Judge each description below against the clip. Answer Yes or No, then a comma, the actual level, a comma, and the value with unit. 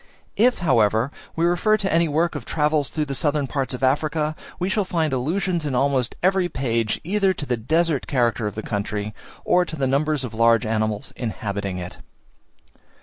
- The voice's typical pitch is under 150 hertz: Yes, medium, 140 Hz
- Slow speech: No, average, 185 wpm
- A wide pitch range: Yes, wide, 6.1 semitones